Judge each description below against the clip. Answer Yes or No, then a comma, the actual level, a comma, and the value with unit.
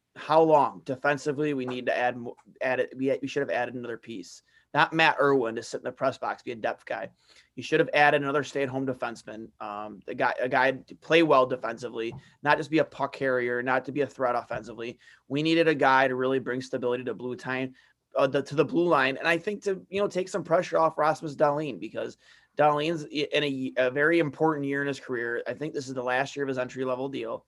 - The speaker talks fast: Yes, fast, 235 wpm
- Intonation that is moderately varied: Yes, average, 3.0 semitones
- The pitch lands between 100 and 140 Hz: Yes, low, 135 Hz